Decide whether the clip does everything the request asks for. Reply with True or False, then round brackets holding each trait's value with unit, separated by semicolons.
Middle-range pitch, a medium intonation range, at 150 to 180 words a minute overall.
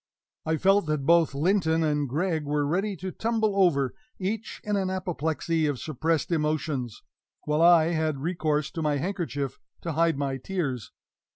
True (160 Hz; 3.8 semitones; 160 wpm)